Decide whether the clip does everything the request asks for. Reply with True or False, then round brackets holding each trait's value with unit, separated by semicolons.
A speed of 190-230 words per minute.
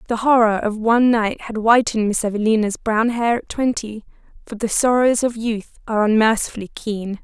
False (175 wpm)